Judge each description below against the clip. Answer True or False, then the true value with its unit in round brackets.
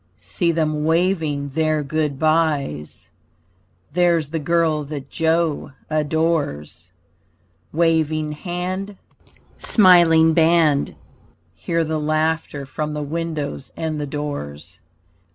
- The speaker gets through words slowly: True (100 wpm)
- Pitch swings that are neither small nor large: False (2.1 semitones)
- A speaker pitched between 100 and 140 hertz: False (155 Hz)